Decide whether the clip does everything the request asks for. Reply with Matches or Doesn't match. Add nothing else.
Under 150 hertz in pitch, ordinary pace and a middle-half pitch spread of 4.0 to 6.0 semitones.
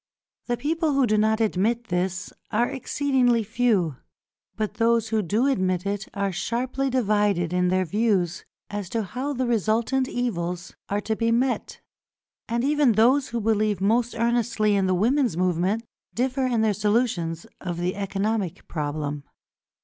Doesn't match